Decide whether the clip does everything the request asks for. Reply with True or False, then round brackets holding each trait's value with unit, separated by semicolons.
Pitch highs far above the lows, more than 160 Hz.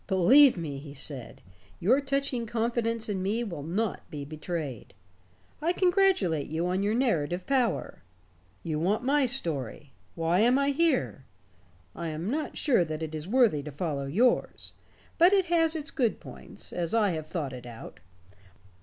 True (8.8 semitones; 190 Hz)